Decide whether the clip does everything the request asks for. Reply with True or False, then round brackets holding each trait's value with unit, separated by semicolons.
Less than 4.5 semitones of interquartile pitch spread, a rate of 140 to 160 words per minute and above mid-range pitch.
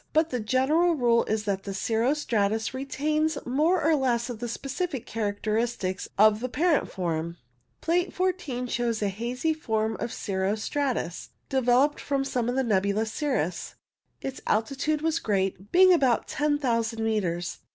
False (5.3 semitones; 150 wpm; 245 Hz)